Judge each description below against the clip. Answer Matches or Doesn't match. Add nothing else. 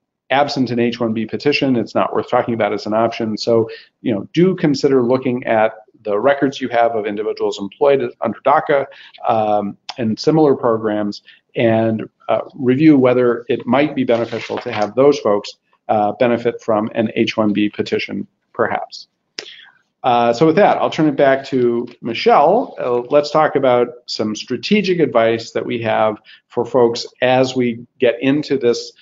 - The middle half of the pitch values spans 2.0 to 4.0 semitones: Matches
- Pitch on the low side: Matches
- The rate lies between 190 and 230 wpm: Doesn't match